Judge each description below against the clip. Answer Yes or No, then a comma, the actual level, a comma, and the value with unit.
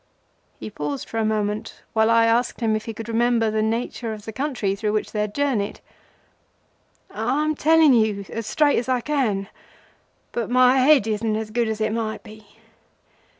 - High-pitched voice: Yes, high, 225 Hz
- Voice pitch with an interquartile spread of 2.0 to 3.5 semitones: Yes, narrow, 2.5 semitones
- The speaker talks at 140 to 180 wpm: No, average, 190 wpm